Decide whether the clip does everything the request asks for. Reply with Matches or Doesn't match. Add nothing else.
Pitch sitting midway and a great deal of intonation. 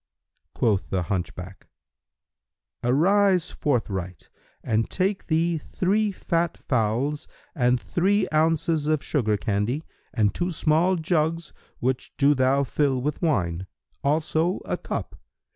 Matches